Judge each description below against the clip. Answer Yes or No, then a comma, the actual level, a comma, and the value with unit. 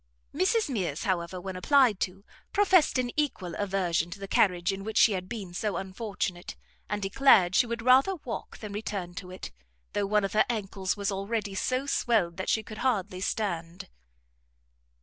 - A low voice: No, high, 200 Hz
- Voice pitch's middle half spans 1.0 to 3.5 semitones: No, average, 3.9 semitones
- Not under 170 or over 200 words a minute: Yes, average, 175 wpm